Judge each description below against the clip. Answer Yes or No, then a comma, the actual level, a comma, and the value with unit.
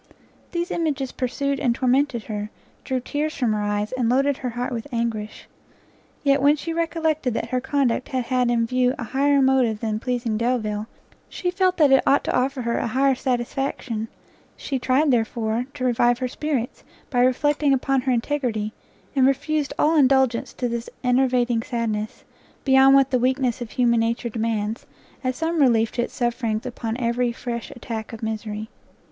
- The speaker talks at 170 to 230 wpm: Yes, average, 175 wpm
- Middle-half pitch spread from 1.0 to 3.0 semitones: Yes, average, 2.7 semitones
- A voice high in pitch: Yes, very high, 250 Hz